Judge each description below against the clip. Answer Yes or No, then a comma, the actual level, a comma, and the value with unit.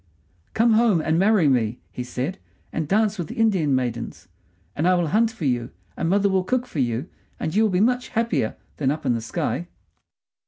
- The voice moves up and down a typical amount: No, wide, 8.5 semitones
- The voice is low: No, medium, 170 Hz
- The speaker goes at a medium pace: No, fast, 210 wpm